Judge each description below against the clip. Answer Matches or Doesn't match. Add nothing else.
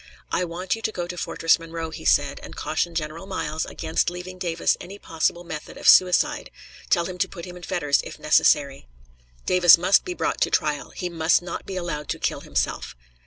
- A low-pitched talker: Doesn't match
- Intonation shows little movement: Matches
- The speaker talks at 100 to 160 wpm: Doesn't match